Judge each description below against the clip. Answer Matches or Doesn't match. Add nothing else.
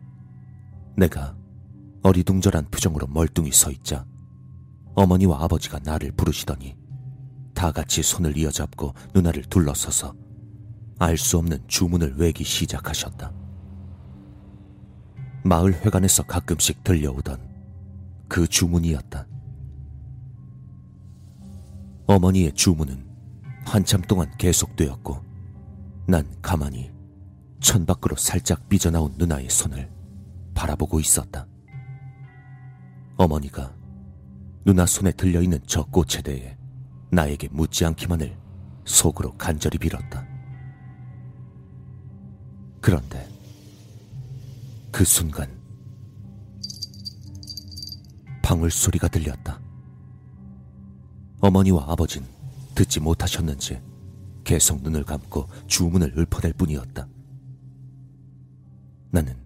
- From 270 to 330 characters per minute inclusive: Doesn't match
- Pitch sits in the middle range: Doesn't match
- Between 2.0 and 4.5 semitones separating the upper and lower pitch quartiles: Doesn't match